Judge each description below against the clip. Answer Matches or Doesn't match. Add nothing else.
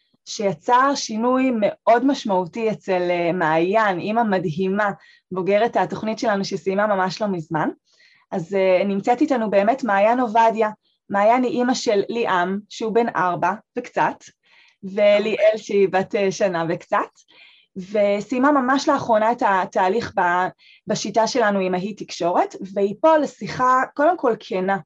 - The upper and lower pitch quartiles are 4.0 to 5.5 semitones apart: Matches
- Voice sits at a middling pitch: Doesn't match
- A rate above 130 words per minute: Doesn't match